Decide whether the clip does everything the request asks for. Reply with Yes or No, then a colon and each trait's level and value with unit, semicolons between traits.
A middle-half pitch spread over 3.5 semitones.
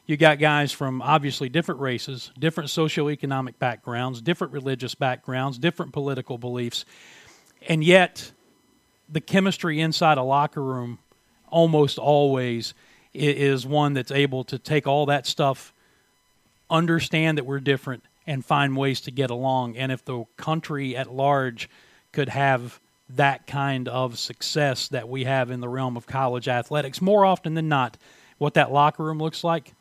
No: average, 3.2 semitones